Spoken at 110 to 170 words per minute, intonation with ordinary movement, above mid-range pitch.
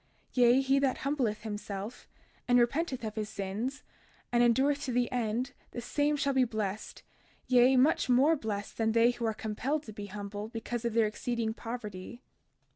No: average, 180 wpm; average, 3.4 semitones; high, 240 Hz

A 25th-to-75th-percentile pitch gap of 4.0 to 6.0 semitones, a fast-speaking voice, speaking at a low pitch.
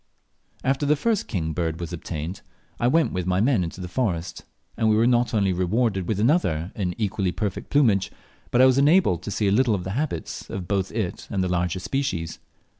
Yes: wide, 5.5 semitones; fast, 210 wpm; low, 100 Hz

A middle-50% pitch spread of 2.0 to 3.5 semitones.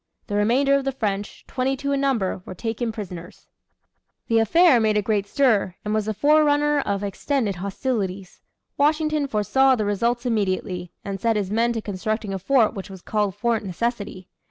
No: average, 5.0 semitones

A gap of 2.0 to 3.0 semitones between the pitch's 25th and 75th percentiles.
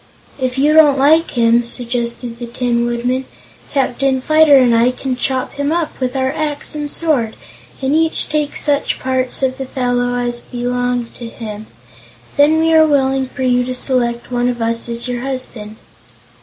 Yes: average, 2.7 semitones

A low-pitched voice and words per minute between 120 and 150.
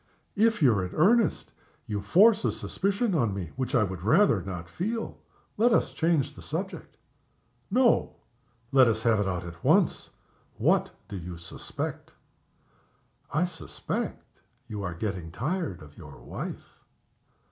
Yes: low, 115 Hz; average, 145 wpm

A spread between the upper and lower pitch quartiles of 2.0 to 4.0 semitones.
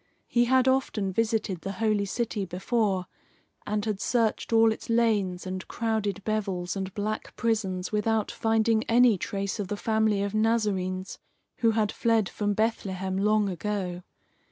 Yes: narrow, 2.6 semitones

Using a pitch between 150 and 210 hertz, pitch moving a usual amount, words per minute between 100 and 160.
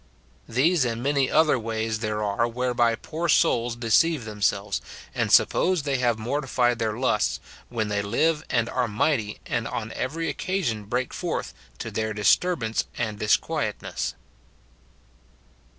No: low, 120 Hz; average, 4.1 semitones; average, 145 wpm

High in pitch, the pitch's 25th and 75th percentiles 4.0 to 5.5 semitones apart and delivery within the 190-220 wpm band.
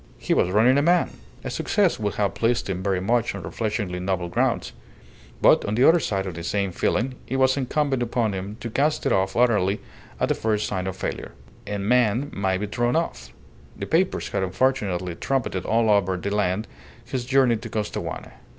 No: low, 105 Hz; average, 4.5 semitones; average, 195 wpm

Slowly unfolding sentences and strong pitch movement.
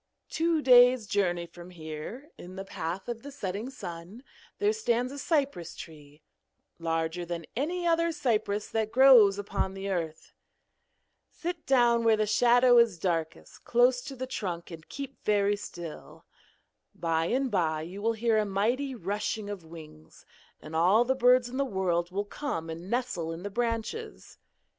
No: average, 160 wpm; wide, 6.5 semitones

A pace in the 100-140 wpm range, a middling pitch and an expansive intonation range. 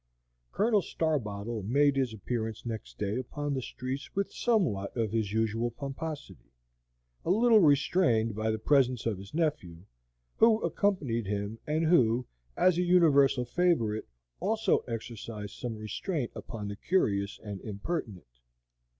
No: slow, 135 wpm; low, 120 Hz; wide, 6.7 semitones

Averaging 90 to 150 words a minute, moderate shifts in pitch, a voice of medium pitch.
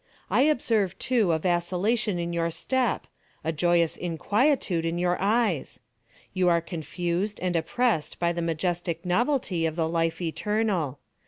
Yes: average, 140 wpm; average, 3.9 semitones; medium, 175 Hz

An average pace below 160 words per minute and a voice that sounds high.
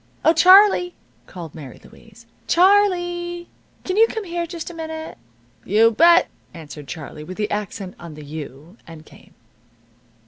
Yes: average, 145 wpm; very high, 315 Hz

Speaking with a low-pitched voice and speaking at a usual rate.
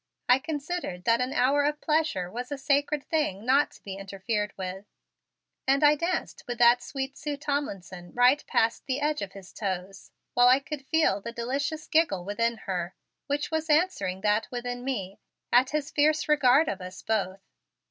No: very high, 250 Hz; average, 180 wpm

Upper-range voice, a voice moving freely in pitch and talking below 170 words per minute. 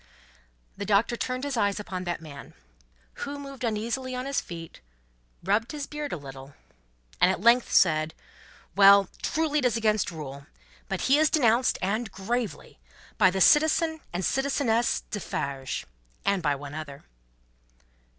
Yes: high, 210 Hz; wide, 6.9 semitones; average, 150 wpm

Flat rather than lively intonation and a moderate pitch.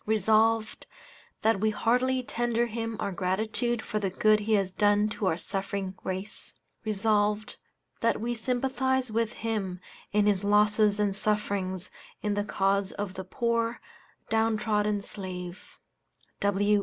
No: narrow, 2.3 semitones; high, 210 Hz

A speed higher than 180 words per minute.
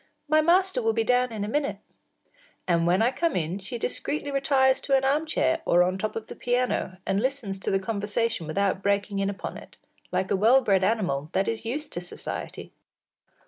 Yes: fast, 205 wpm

